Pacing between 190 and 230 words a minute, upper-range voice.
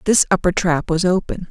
No: average, 200 wpm; medium, 175 Hz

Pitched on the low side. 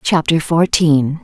No: medium, 155 Hz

